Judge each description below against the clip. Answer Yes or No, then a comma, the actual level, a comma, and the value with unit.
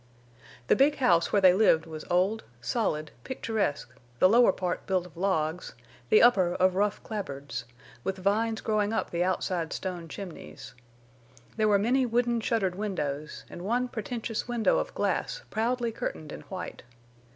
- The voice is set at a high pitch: Yes, high, 195 Hz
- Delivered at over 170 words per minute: No, average, 155 wpm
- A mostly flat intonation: No, average, 4.6 semitones